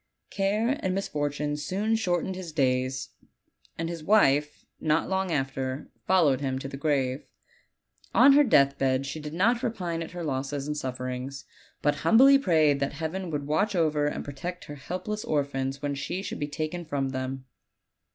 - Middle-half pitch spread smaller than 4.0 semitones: No, average, 4.9 semitones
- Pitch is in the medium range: Yes, medium, 150 Hz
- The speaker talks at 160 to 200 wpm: Yes, average, 170 wpm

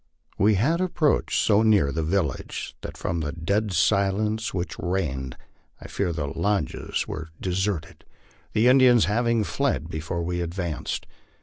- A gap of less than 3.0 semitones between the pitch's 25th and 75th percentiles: No, average, 4.8 semitones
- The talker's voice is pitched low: Yes, very low, 95 Hz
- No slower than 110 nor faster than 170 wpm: Yes, average, 145 wpm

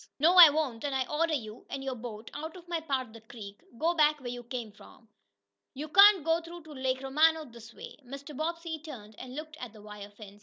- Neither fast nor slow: No, fast, 235 wpm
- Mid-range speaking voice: No, very high, 275 Hz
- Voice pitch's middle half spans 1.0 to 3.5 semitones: No, wide, 5.4 semitones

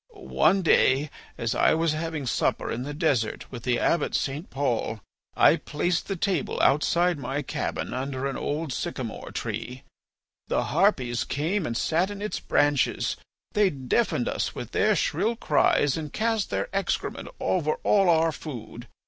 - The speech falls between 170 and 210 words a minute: No, average, 155 wpm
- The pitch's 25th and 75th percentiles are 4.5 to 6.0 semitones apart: Yes, average, 4.9 semitones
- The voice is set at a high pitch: No, medium, 150 Hz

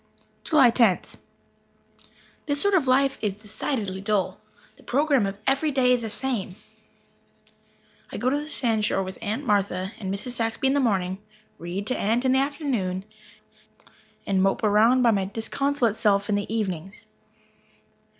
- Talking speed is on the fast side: No, average, 155 wpm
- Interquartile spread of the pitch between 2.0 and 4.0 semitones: No, average, 5.1 semitones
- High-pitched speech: Yes, high, 225 Hz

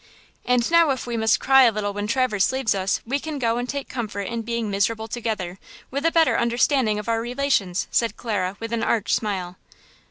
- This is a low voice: No, high, 230 Hz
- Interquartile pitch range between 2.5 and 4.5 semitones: Yes, average, 3.5 semitones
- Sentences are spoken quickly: Yes, fast, 210 wpm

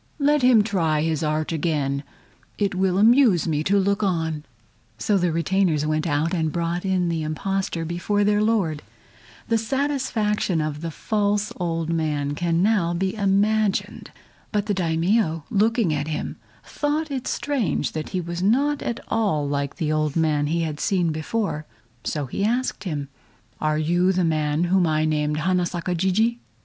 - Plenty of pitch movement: No, average, 4.9 semitones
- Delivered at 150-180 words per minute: Yes, average, 165 wpm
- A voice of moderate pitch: Yes, medium, 175 Hz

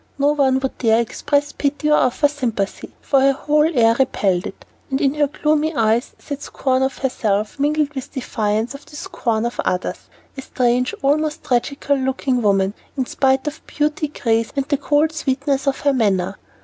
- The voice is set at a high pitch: Yes, very high, 270 Hz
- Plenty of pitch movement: No, average, 3.7 semitones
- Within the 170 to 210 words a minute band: Yes, average, 180 wpm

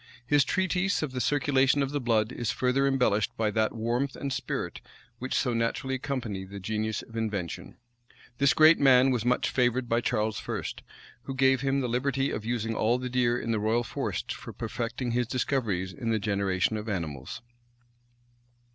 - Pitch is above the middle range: No, low, 120 Hz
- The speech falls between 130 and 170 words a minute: No, average, 180 wpm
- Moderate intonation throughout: Yes, average, 3.4 semitones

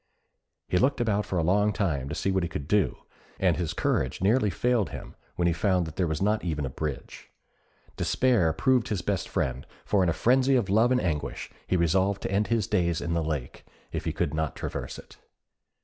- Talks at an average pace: No, fast, 215 wpm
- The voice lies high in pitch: No, very low, 90 Hz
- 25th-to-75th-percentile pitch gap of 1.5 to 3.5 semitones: No, average, 4.8 semitones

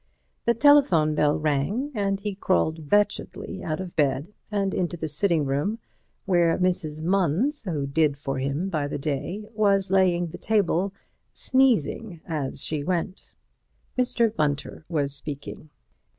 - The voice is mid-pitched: Yes, medium, 175 Hz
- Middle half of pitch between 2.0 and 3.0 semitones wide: No, average, 5.0 semitones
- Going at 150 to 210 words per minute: No, average, 140 wpm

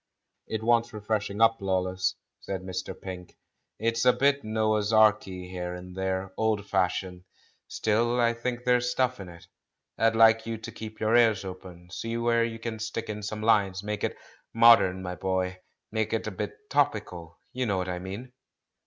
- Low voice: Yes, low, 110 Hz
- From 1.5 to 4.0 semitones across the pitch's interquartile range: Yes, average, 3.5 semitones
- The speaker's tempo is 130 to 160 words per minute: No, average, 180 wpm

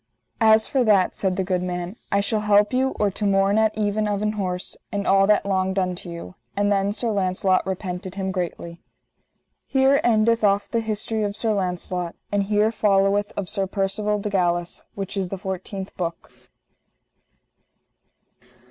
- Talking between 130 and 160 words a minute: No, average, 170 wpm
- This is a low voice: No, high, 200 Hz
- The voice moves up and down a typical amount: No, narrow, 2.1 semitones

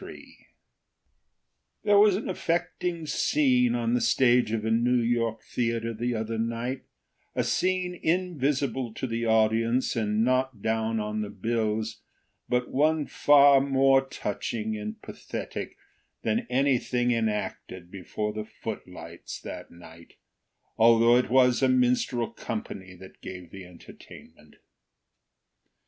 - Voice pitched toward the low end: Yes, low, 115 Hz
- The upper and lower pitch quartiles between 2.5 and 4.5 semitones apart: Yes, average, 3.4 semitones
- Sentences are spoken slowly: Yes, slow, 125 wpm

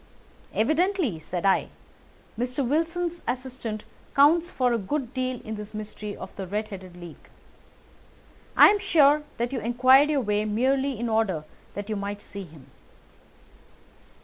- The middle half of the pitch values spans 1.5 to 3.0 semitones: No, average, 5.1 semitones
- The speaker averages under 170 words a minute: Yes, average, 150 wpm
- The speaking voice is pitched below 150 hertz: No, high, 235 Hz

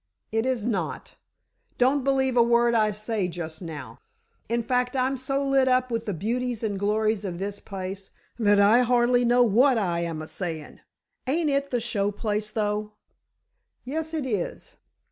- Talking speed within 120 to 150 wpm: No, average, 170 wpm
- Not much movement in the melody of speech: No, average, 3.8 semitones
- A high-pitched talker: Yes, high, 225 Hz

